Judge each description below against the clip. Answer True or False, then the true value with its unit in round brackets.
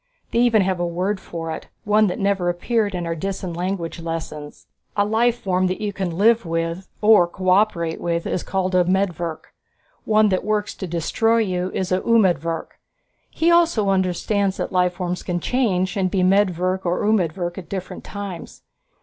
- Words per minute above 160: True (170 wpm)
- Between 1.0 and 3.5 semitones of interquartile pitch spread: True (2.9 semitones)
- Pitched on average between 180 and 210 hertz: True (185 Hz)